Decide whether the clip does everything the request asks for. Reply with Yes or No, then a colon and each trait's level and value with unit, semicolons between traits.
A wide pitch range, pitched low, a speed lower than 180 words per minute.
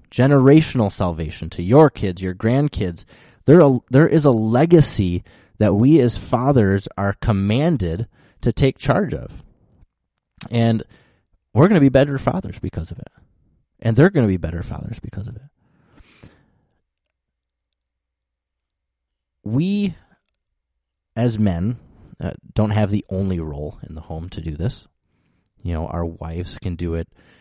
Yes: wide, 7.1 semitones; low, 100 Hz; average, 140 wpm